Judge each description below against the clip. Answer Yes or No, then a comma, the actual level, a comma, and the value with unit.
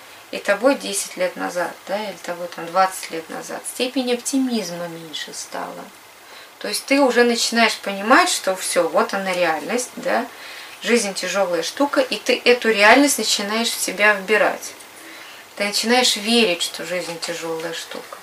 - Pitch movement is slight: No, average, 4.7 semitones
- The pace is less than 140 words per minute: No, average, 150 wpm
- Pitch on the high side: Yes, high, 215 Hz